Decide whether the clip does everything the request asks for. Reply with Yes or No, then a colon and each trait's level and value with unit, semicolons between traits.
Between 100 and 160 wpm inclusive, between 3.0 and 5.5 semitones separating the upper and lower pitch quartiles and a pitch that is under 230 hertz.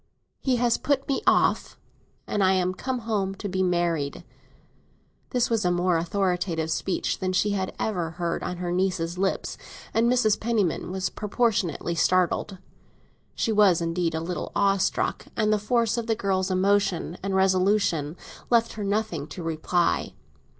Yes: average, 155 wpm; average, 3.4 semitones; high, 190 Hz